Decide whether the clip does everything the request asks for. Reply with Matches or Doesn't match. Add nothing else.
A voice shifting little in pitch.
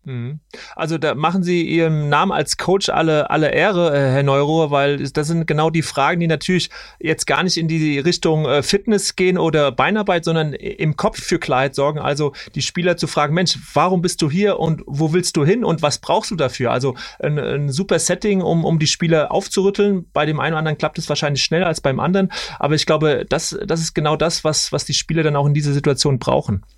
Doesn't match